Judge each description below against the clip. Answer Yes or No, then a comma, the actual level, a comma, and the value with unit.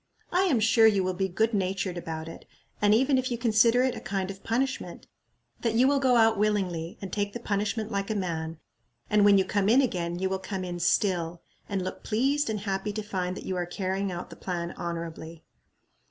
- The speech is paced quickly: Yes, fast, 220 wpm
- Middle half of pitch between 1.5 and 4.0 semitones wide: Yes, average, 3.7 semitones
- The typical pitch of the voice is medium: No, high, 200 Hz